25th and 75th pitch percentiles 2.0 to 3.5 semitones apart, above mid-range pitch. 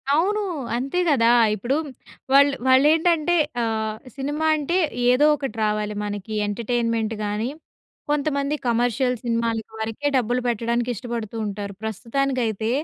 No: average, 4.1 semitones; high, 240 Hz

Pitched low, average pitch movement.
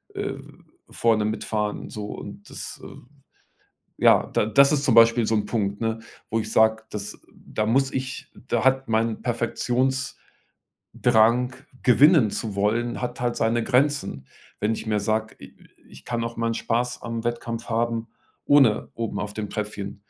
No: low, 115 Hz; narrow, 2.3 semitones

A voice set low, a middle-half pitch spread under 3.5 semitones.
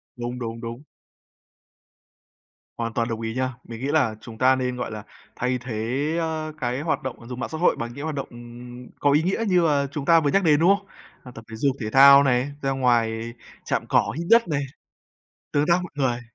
No: low, 130 Hz; average, 3.8 semitones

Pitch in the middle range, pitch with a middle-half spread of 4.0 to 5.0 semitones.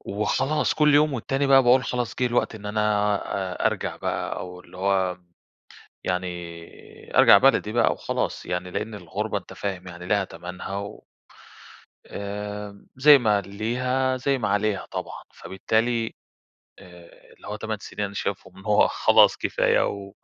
No: low, 105 Hz; average, 4.3 semitones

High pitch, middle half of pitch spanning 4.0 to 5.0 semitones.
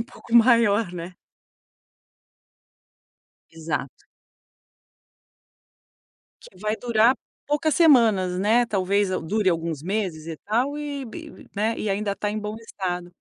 Yes: high, 210 Hz; average, 4.4 semitones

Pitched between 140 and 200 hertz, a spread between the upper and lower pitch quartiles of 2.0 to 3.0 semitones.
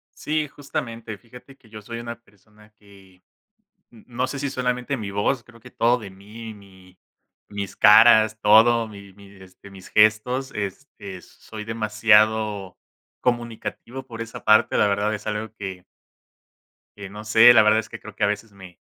No: low, 110 Hz; narrow, 2.5 semitones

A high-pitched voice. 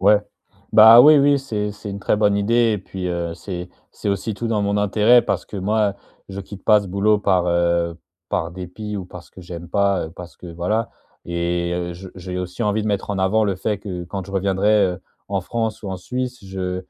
No: low, 100 Hz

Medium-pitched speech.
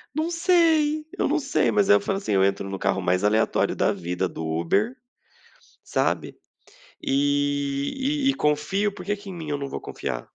Yes: medium, 165 Hz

